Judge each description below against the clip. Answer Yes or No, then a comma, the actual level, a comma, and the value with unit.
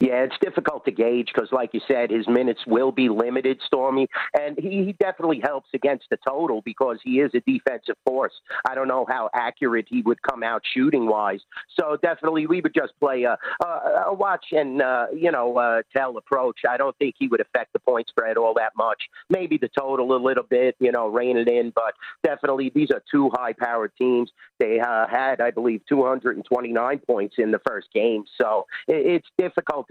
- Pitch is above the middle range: No, low, 130 Hz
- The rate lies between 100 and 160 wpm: No, average, 195 wpm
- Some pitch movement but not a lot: Yes, average, 3.6 semitones